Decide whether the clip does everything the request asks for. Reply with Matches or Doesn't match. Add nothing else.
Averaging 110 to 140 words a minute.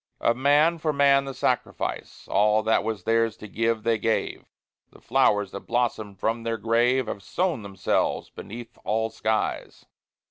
Doesn't match